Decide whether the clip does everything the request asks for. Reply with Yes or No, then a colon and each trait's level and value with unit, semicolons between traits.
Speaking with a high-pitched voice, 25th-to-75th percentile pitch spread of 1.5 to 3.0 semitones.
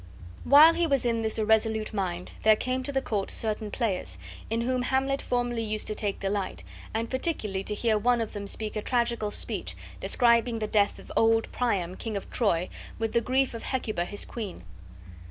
Yes: high, 225 Hz; average, 2.7 semitones